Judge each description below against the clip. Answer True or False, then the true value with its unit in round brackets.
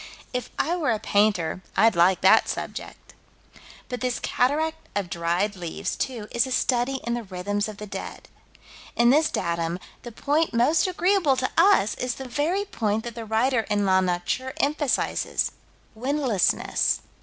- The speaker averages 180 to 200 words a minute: False (160 wpm)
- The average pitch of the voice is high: True (235 Hz)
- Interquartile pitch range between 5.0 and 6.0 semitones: True (5.3 semitones)